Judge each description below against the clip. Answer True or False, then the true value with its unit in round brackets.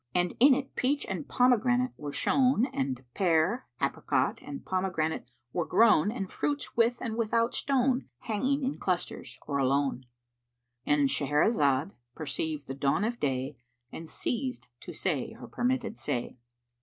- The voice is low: False (185 Hz)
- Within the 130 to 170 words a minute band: True (140 wpm)